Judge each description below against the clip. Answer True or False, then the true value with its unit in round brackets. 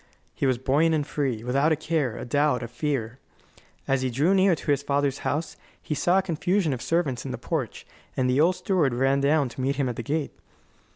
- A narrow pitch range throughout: False (3.5 semitones)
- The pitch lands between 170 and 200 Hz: False (140 Hz)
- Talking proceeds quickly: True (225 wpm)